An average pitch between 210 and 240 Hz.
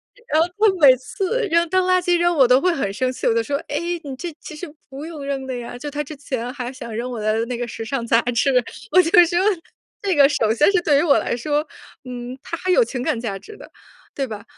No: very high, 275 Hz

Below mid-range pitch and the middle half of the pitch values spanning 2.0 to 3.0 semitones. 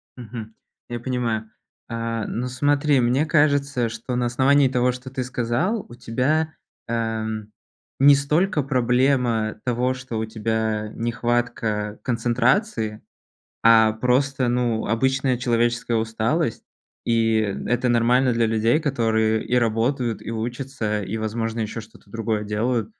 Yes: low, 120 Hz; narrow, 2.4 semitones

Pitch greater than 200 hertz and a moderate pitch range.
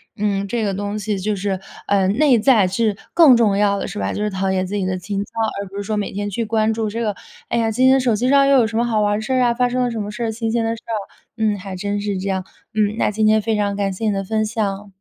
No: high, 210 Hz; narrow, 2.3 semitones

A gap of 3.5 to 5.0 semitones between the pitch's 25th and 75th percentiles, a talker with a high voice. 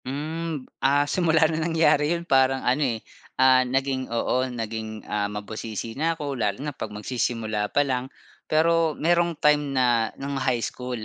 No: average, 4.6 semitones; low, 135 Hz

